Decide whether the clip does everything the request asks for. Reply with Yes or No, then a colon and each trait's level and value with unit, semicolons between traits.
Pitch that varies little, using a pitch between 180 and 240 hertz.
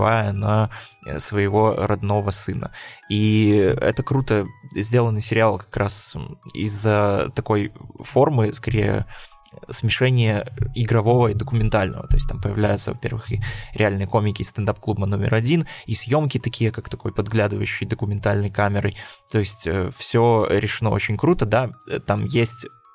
No: narrow, 2.3 semitones; low, 110 Hz